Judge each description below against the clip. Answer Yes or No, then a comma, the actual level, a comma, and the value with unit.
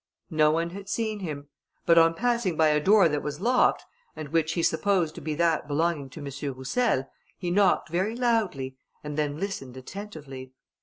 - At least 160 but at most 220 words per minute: Yes, average, 185 wpm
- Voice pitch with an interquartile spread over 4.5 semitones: Yes, average, 5.2 semitones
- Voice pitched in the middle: Yes, medium, 165 Hz